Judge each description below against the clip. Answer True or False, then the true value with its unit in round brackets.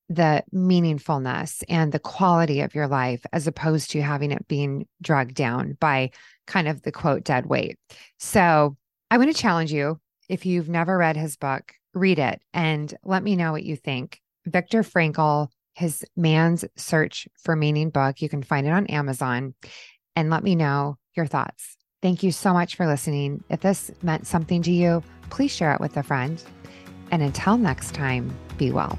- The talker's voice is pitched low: False (155 Hz)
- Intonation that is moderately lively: True (3.5 semitones)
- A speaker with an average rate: True (180 wpm)